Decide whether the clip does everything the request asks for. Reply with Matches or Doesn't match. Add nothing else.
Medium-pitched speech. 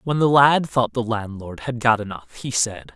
Doesn't match